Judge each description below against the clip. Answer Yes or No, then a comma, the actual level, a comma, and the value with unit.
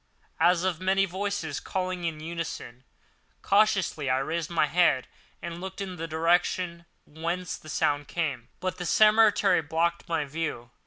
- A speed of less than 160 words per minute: Yes, average, 150 wpm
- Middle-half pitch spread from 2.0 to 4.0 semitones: Yes, average, 2.9 semitones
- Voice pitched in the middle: Yes, medium, 170 Hz